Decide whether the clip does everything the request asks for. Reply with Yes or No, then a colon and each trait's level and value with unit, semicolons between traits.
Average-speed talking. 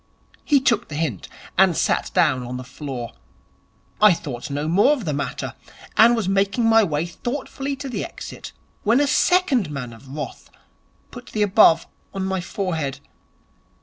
Yes: average, 165 wpm